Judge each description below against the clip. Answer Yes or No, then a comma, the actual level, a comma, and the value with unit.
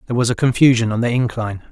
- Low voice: Yes, low, 115 Hz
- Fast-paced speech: Yes, fast, 245 wpm